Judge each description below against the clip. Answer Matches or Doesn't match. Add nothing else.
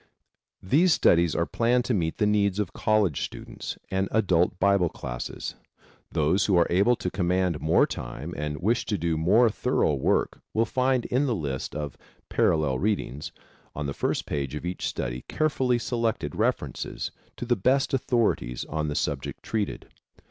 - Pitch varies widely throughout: Matches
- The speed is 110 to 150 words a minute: Doesn't match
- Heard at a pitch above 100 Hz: Doesn't match